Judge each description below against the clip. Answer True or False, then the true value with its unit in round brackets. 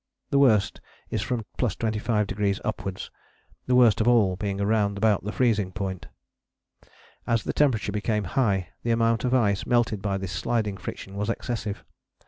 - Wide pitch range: False (2.7 semitones)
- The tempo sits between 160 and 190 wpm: False (150 wpm)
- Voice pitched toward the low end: True (105 Hz)